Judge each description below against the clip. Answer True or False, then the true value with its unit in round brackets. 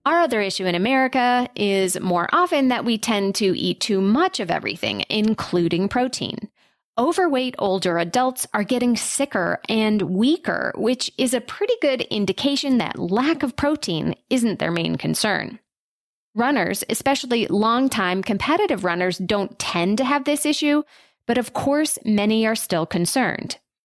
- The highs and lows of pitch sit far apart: True (5.9 semitones)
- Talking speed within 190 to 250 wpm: False (150 wpm)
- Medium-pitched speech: False (230 Hz)